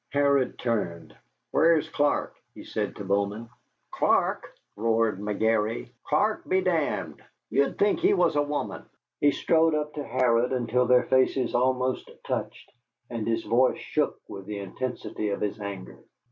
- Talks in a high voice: No, low, 125 Hz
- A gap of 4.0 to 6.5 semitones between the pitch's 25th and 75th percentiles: Yes, average, 5.0 semitones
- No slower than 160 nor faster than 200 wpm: No, average, 150 wpm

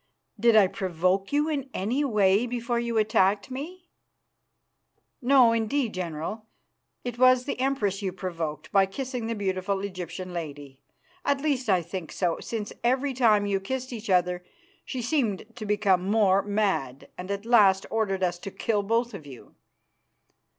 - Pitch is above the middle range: Yes, high, 205 Hz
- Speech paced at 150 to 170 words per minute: Yes, average, 155 wpm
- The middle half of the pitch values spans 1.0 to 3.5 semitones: No, average, 4.5 semitones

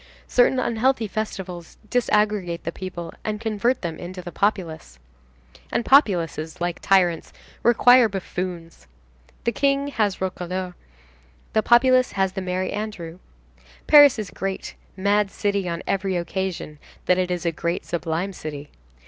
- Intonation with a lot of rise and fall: No, average, 3.9 semitones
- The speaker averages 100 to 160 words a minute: Yes, average, 140 wpm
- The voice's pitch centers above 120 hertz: Yes, high, 190 Hz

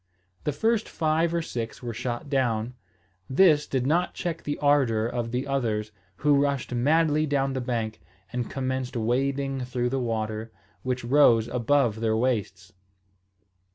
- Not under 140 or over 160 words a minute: Yes, average, 150 wpm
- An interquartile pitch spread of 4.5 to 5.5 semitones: No, average, 3.7 semitones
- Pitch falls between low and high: No, low, 130 Hz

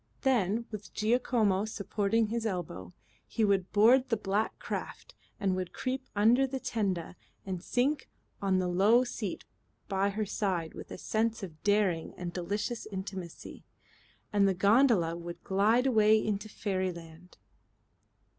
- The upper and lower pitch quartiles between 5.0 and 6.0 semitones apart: No, average, 3.4 semitones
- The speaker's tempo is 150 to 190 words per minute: No, average, 140 wpm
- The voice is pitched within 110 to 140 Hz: No, high, 205 Hz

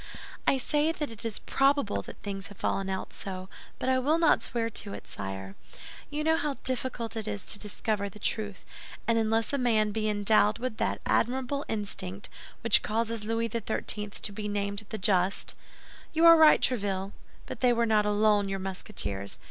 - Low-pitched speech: No, high, 215 Hz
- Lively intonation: No, average, 3.3 semitones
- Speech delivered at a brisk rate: No, average, 185 wpm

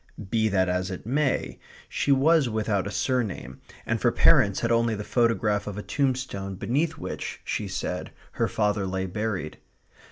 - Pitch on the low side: Yes, low, 105 Hz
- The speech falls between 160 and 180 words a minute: Yes, average, 165 wpm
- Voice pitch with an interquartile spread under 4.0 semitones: No, average, 4.3 semitones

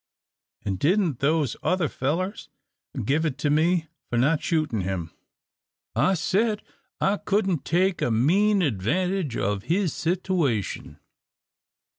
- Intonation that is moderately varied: No, wide, 6.4 semitones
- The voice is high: No, medium, 160 Hz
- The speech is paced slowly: Yes, slow, 120 wpm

